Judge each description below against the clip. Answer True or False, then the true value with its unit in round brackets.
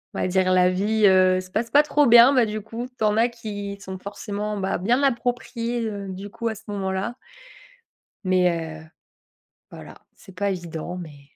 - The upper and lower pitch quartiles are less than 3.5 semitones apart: False (3.8 semitones)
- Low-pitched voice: False (205 Hz)